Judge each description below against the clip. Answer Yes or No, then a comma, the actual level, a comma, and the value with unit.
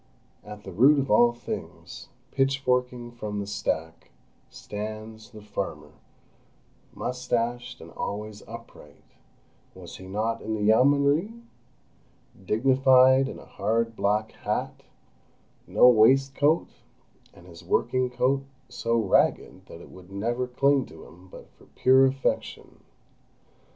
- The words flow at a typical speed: No, slow, 115 wpm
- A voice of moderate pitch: No, low, 115 Hz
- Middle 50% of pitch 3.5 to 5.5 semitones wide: Yes, average, 4.0 semitones